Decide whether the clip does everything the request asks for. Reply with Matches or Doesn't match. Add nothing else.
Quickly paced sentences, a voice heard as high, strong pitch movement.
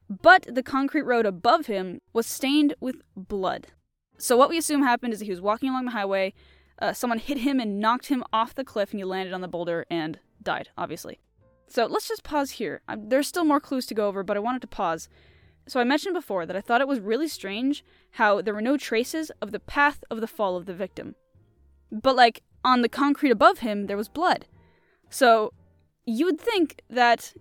Matches